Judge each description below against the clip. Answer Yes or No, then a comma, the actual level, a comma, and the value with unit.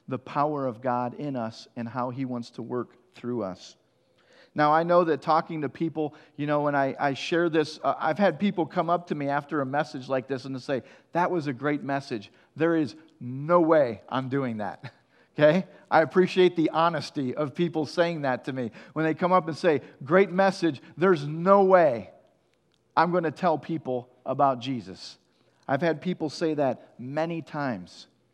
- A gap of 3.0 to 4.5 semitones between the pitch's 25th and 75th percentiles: Yes, average, 4.1 semitones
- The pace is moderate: Yes, average, 195 wpm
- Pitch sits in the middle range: Yes, medium, 150 Hz